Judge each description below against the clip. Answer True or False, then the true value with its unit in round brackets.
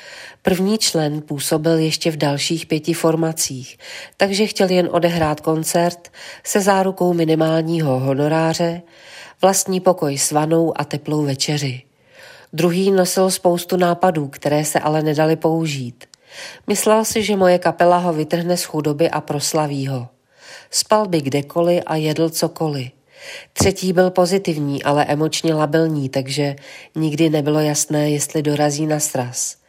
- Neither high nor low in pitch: True (160 Hz)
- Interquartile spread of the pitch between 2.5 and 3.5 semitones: True (2.9 semitones)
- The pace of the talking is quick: False (130 wpm)